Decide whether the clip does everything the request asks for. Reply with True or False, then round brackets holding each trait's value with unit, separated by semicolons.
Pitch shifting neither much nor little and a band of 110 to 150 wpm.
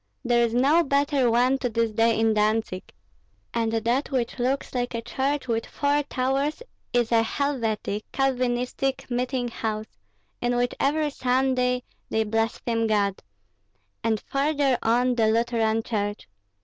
True (3.0 semitones; 140 wpm)